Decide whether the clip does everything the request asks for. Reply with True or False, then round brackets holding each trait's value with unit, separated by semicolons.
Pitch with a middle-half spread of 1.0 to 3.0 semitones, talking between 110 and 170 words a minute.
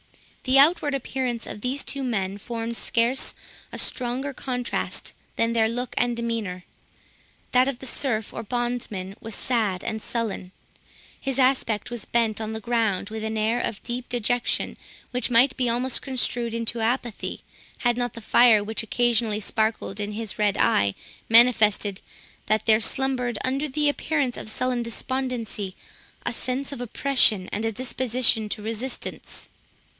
True (2.6 semitones; 155 wpm)